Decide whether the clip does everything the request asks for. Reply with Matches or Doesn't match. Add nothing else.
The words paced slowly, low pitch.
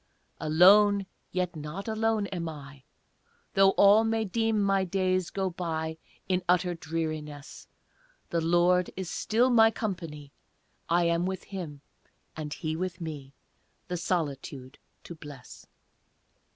Doesn't match